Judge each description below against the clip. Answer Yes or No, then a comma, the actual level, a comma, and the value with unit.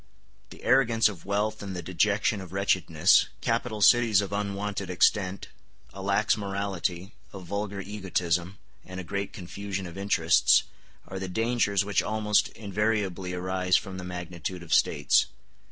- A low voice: Yes, low, 100 Hz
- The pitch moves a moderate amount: No, narrow, 2.1 semitones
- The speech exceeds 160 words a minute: No, average, 145 wpm